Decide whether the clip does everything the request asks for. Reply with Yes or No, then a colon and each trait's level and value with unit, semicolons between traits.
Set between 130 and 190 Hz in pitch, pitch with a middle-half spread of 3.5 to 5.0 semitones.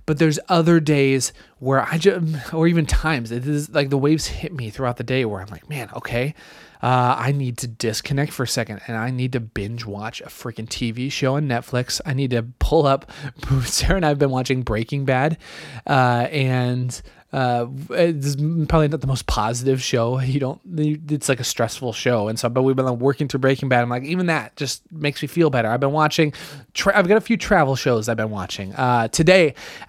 Yes: low, 135 Hz; average, 3.9 semitones